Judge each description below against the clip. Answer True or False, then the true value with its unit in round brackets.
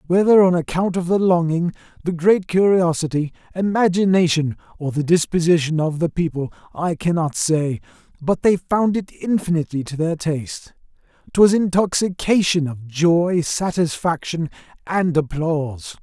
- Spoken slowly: True (125 wpm)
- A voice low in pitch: False (170 Hz)